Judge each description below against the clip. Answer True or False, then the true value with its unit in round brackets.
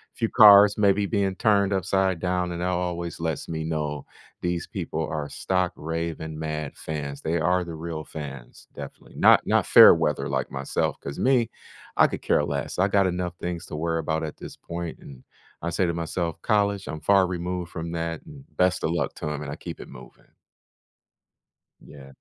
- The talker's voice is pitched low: True (85 Hz)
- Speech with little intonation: False (3.1 semitones)